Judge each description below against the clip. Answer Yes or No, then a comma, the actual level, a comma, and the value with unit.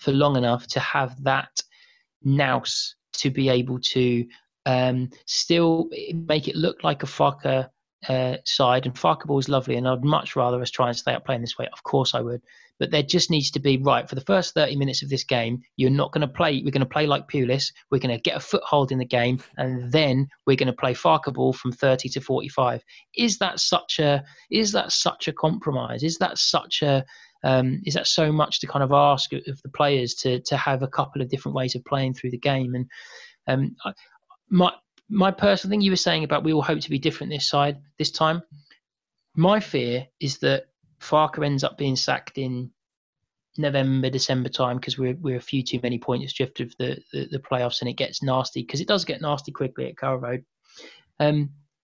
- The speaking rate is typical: No, fast, 220 wpm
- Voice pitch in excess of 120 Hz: Yes, medium, 140 Hz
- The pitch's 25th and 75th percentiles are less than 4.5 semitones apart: Yes, average, 3.0 semitones